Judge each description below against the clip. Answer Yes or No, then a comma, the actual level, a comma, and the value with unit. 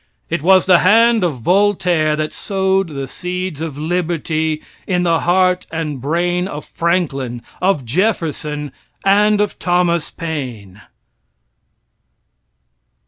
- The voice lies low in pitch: No, medium, 170 Hz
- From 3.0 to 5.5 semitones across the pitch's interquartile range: Yes, average, 3.5 semitones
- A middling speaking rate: No, slow, 115 wpm